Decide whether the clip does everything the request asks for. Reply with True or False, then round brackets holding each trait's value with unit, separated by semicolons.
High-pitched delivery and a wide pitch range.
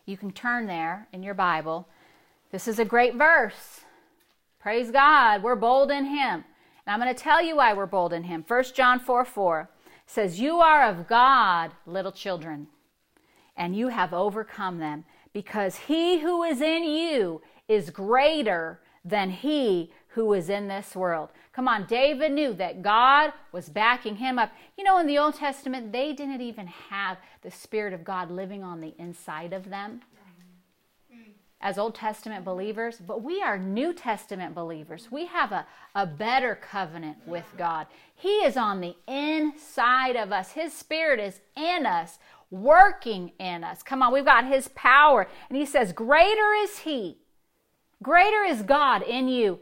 True (225 Hz; 7.0 semitones)